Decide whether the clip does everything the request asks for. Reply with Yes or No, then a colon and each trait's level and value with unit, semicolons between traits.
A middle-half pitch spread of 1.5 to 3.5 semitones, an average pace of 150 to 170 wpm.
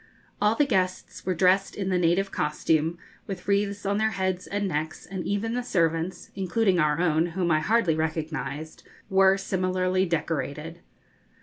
Yes: average, 3.2 semitones; average, 160 wpm